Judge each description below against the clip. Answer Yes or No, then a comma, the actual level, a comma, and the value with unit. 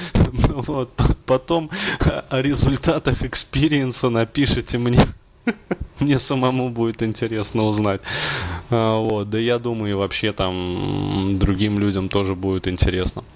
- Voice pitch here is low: Yes, low, 115 Hz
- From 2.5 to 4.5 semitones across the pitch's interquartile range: No, average, 4.9 semitones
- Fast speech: No, slow, 110 wpm